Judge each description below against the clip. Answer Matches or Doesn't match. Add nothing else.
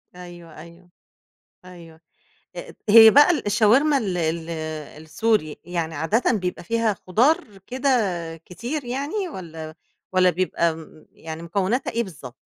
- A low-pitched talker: Doesn't match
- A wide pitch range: Matches